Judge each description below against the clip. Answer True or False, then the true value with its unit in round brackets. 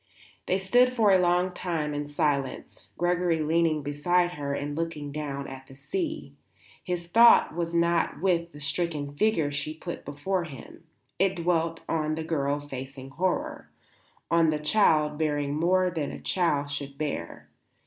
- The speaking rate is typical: True (160 wpm)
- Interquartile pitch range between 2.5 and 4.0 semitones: True (3.4 semitones)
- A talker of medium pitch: True (160 Hz)